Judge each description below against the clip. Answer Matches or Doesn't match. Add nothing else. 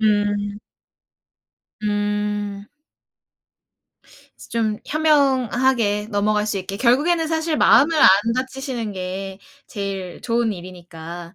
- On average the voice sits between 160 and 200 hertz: Doesn't match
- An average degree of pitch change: Matches